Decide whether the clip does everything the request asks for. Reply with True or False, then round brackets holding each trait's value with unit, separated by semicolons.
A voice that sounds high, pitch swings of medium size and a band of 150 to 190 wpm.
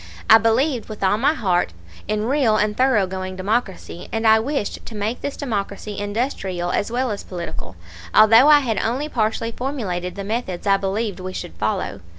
True (215 Hz; 4.0 semitones; 175 wpm)